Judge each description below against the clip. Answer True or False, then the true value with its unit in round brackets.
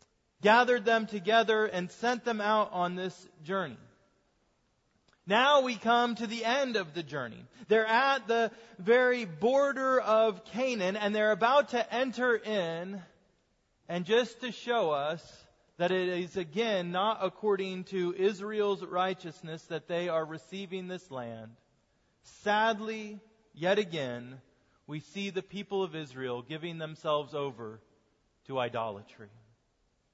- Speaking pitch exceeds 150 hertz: True (190 Hz)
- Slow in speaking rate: True (130 wpm)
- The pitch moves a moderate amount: False (6.0 semitones)